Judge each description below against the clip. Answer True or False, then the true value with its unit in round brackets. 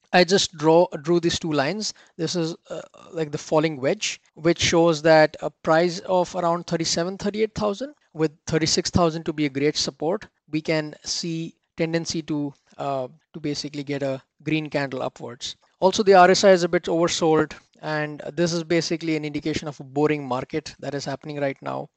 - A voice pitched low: False (160 Hz)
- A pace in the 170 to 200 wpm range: True (180 wpm)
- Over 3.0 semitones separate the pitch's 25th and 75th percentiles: False (2.4 semitones)